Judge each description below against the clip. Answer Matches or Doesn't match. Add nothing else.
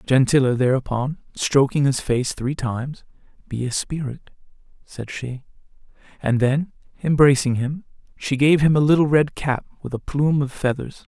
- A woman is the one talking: Doesn't match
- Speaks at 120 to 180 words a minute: Matches